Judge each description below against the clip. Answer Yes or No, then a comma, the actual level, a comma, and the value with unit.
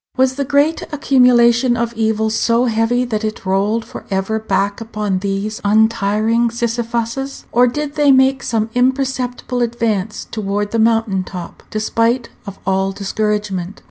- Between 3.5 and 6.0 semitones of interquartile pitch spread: No, average, 2.9 semitones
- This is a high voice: Yes, high, 225 Hz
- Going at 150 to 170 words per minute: No, average, 140 wpm